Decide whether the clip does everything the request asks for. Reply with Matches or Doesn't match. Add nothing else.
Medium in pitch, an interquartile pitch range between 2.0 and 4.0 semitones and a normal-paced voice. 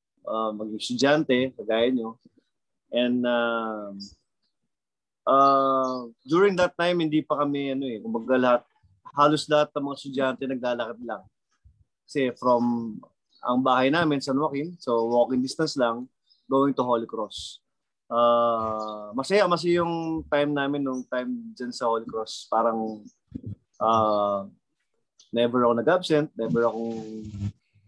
Doesn't match